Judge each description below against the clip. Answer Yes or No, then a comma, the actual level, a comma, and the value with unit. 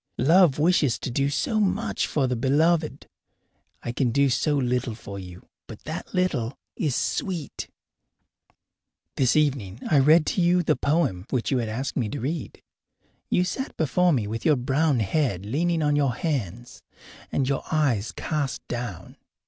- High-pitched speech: No, medium, 140 Hz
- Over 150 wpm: Yes, average, 165 wpm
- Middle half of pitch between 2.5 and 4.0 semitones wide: No, average, 4.8 semitones